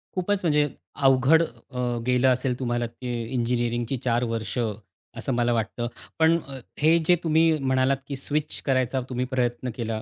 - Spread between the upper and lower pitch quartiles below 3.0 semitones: Yes, narrow, 2.6 semitones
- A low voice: Yes, low, 130 Hz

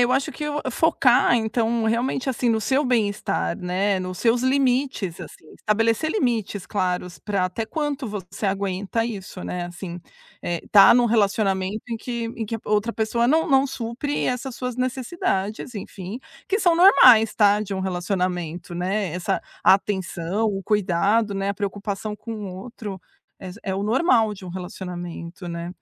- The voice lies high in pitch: Yes, high, 210 Hz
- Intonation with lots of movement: No, average, 4.1 semitones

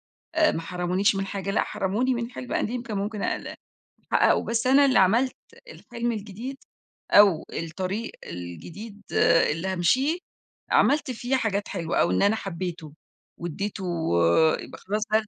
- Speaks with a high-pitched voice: Yes, high, 205 Hz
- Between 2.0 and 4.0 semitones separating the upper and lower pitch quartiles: No, average, 4.6 semitones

